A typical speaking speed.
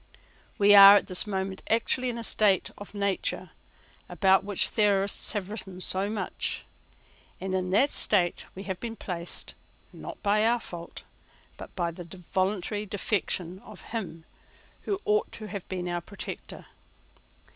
Yes: average, 150 wpm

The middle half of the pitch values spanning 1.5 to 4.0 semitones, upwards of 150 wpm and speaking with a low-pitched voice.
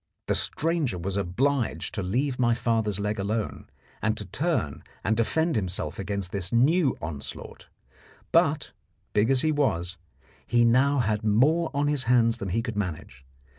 No: wide, 5.4 semitones; average, 160 wpm; low, 115 Hz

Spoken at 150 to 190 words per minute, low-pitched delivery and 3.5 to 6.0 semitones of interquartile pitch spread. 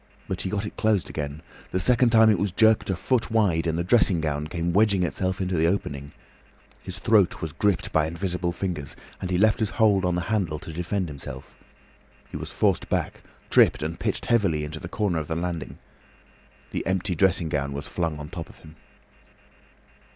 No: average, 200 wpm; very low, 90 Hz; average, 4.0 semitones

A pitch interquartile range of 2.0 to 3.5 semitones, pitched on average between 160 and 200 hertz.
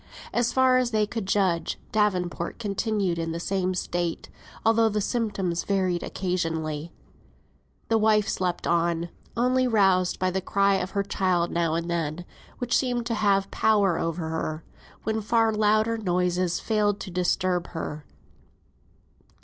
No: average, 3.9 semitones; high, 190 Hz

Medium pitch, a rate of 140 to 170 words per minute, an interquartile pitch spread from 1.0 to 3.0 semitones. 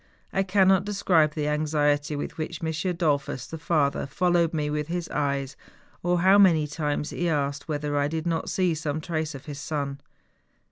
No: medium, 155 Hz; average, 180 wpm; average, 2.7 semitones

